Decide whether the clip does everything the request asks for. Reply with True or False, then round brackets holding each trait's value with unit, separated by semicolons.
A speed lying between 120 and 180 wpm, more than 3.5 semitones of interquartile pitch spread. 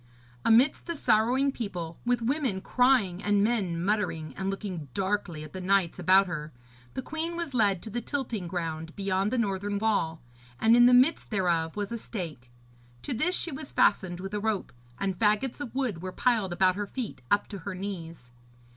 False (190 wpm; 4.8 semitones)